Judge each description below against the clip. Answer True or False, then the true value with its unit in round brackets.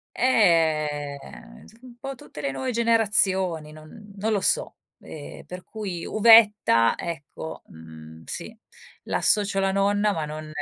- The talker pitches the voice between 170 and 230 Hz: True (190 Hz)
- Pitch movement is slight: False (6.1 semitones)